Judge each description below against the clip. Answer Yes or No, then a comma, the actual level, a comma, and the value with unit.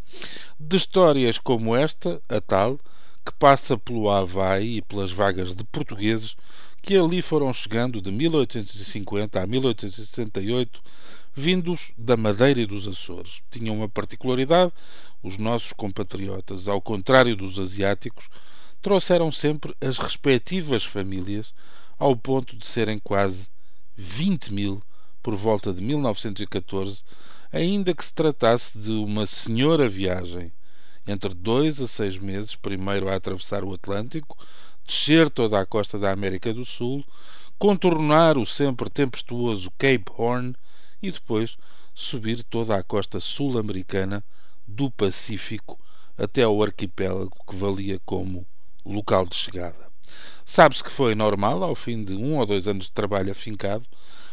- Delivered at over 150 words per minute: No, average, 130 wpm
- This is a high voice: No, low, 110 Hz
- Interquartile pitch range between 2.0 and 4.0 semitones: No, average, 4.8 semitones